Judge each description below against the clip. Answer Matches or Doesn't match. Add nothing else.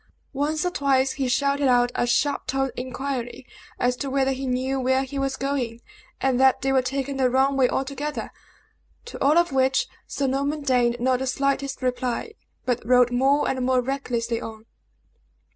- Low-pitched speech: Doesn't match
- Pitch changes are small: Matches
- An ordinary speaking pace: Matches